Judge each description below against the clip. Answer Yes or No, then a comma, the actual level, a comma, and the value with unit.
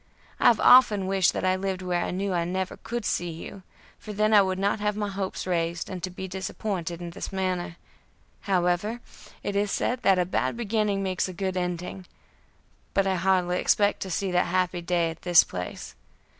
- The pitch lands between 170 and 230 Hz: Yes, medium, 185 Hz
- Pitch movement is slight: Yes, narrow, 2.1 semitones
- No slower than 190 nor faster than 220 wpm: Yes, average, 200 wpm